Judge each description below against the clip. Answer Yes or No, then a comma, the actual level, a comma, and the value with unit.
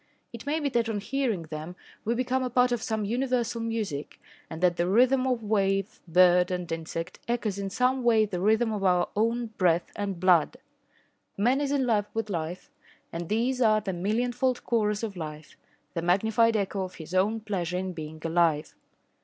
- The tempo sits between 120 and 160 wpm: No, average, 185 wpm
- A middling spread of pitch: Yes, average, 4.8 semitones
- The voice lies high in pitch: Yes, high, 210 Hz